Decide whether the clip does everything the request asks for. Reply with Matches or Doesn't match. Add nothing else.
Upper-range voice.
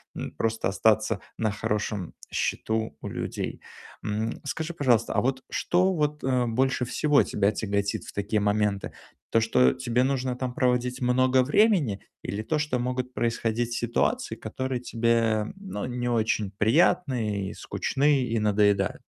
Doesn't match